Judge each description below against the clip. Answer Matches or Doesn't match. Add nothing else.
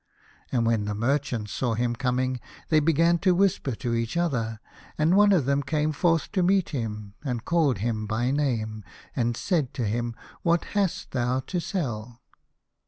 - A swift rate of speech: Doesn't match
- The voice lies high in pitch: Doesn't match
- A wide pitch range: Matches